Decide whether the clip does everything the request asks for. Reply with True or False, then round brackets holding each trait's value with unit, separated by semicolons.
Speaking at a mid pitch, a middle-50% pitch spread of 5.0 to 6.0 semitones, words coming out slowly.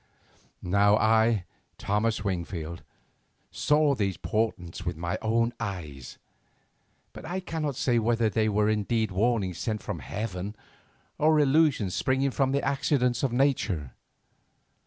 False (110 Hz; 5.6 semitones; 125 wpm)